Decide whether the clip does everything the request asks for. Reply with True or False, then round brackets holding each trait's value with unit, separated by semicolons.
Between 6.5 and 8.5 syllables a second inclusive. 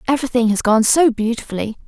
True (6.7 syllables/s)